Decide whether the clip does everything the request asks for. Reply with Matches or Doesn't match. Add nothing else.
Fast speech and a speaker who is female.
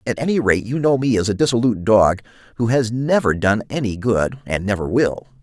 Doesn't match